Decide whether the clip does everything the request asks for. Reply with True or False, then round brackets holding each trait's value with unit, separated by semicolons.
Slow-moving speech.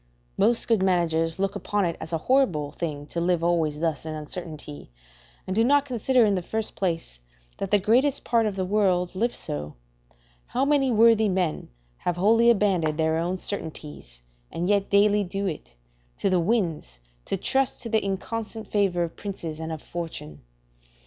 False (175 wpm)